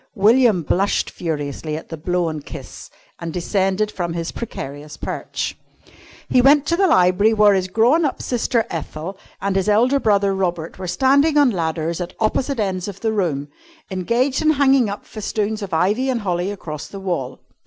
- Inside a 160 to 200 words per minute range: Yes, average, 175 wpm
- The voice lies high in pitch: Yes, high, 195 Hz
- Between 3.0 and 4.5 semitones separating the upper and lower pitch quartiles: No, average, 5.3 semitones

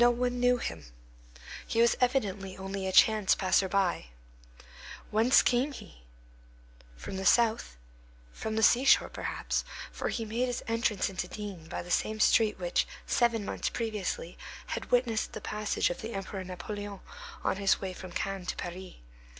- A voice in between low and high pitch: No, high, 210 Hz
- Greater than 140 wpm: Yes, average, 160 wpm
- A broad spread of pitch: No, average, 3.7 semitones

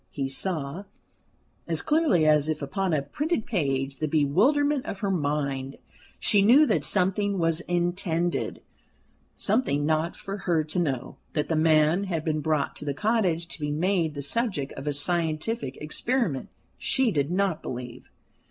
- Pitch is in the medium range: Yes, medium, 165 Hz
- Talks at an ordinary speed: Yes, average, 160 wpm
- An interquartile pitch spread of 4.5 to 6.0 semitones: Yes, average, 5.1 semitones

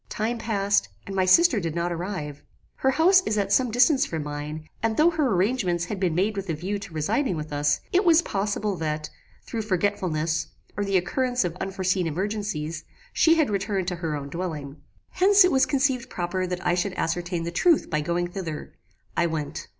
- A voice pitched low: No, high, 190 Hz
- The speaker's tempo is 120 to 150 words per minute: No, average, 195 wpm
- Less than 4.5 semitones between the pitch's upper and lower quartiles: No, average, 5.2 semitones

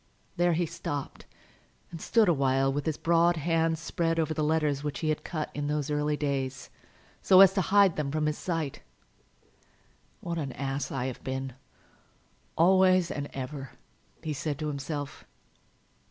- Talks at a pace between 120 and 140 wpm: No, average, 165 wpm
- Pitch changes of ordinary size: Yes, average, 3.1 semitones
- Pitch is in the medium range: Yes, medium, 150 Hz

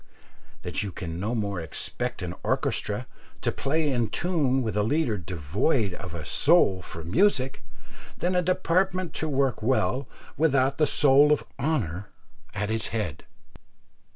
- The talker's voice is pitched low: Yes, low, 130 Hz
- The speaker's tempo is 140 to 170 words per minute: Yes, average, 150 wpm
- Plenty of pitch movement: Yes, wide, 7.6 semitones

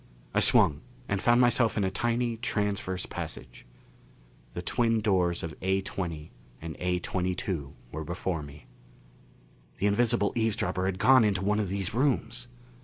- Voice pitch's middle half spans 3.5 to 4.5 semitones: Yes, average, 4.1 semitones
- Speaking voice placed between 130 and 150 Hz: No, very low, 95 Hz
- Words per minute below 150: Yes, average, 140 wpm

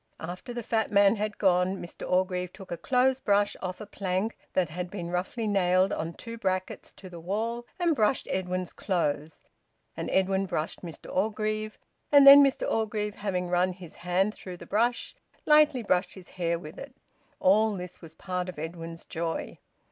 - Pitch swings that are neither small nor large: Yes, average, 3.3 semitones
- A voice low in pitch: No, high, 190 Hz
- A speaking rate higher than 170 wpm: Yes, average, 180 wpm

